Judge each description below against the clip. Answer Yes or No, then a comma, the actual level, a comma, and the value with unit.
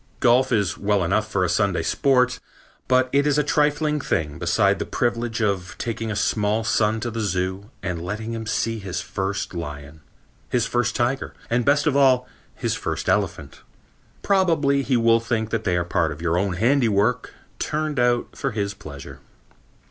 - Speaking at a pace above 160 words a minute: Yes, average, 180 wpm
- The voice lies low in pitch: Yes, low, 110 Hz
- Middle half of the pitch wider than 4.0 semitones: Yes, average, 4.8 semitones